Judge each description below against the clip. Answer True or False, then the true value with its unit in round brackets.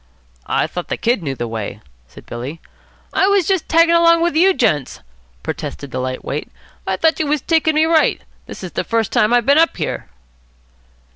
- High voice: True (250 Hz)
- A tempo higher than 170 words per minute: True (200 wpm)